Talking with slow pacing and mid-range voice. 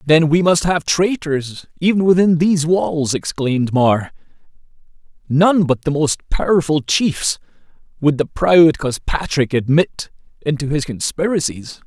Yes: slow, 125 wpm; medium, 155 Hz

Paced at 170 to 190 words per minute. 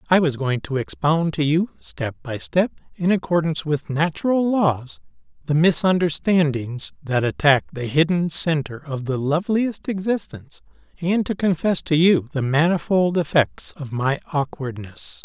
No: average, 145 wpm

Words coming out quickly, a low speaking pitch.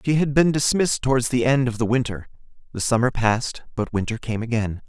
Yes: fast, 210 wpm; low, 120 Hz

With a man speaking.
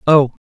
Yes: male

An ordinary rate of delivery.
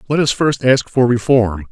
No: fast, 210 wpm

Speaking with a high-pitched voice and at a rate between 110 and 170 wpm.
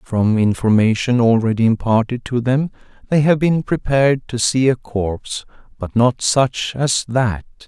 No: low, 120 Hz; average, 150 wpm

